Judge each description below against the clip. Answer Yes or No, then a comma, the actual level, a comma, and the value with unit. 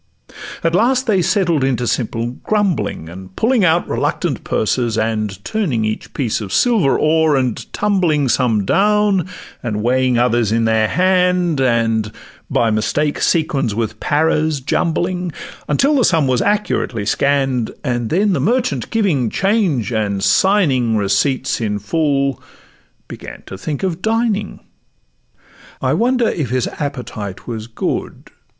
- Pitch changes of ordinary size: No, wide, 8.4 semitones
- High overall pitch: No, medium, 140 Hz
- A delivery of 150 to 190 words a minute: No, slow, 135 wpm